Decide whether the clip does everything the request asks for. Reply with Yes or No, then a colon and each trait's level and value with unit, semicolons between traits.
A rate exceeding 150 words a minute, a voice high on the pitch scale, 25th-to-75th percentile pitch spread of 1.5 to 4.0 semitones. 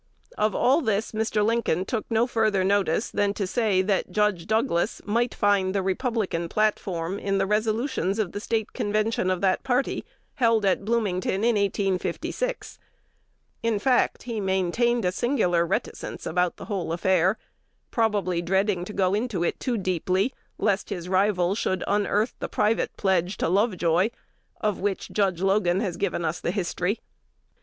Yes: average, 160 wpm; high, 200 Hz; average, 3.0 semitones